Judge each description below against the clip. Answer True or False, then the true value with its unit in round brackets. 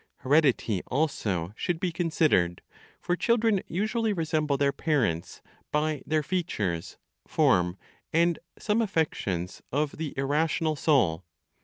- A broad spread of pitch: True (6.6 semitones)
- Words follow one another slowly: True (115 wpm)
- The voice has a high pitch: False (150 Hz)